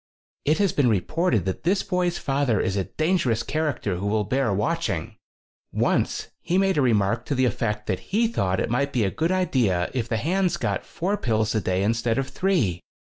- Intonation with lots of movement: Yes, wide, 8.1 semitones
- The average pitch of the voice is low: Yes, low, 125 Hz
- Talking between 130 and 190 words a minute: No, average, 200 wpm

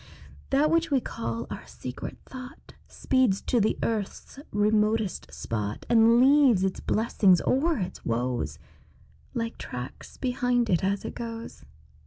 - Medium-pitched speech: No, high, 225 Hz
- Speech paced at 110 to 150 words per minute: Yes, slow, 135 wpm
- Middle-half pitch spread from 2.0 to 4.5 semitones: No, wide, 5.4 semitones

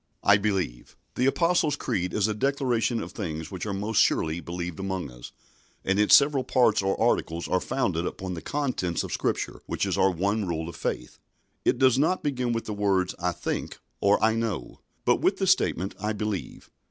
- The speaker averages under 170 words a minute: No, average, 195 wpm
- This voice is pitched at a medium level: No, low, 100 Hz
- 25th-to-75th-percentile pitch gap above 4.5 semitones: Yes, average, 5.1 semitones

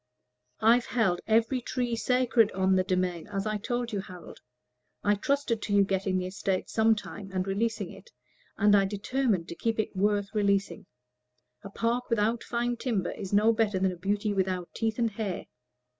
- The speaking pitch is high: Yes, high, 205 Hz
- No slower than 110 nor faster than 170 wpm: No, average, 180 wpm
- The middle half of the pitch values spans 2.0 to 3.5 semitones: Yes, average, 3.1 semitones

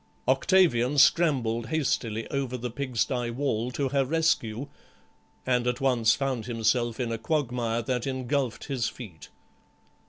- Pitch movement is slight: No, average, 3.0 semitones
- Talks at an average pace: No, slow, 130 wpm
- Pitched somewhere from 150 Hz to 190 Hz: No, low, 125 Hz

